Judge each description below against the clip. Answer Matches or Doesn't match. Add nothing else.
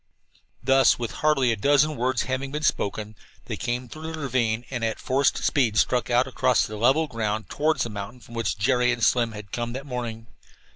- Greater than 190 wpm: Matches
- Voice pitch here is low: Matches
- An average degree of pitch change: Matches